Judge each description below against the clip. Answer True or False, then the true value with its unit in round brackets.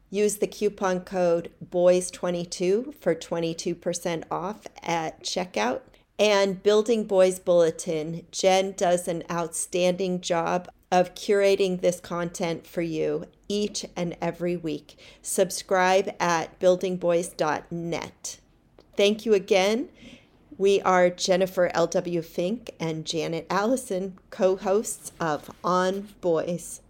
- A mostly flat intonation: True (2.3 semitones)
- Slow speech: True (105 wpm)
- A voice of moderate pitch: True (180 Hz)